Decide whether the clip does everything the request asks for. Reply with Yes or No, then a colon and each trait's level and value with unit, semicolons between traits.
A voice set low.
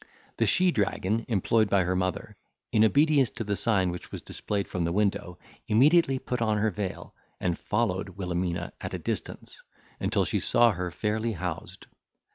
Yes: low, 105 Hz